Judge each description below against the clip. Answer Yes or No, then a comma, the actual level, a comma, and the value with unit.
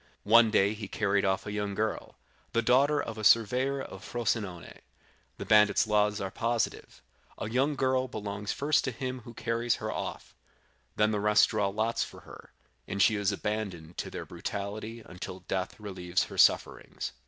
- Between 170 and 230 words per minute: Yes, average, 175 wpm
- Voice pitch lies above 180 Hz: No, low, 110 Hz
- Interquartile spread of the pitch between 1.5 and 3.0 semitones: Yes, narrow, 2.5 semitones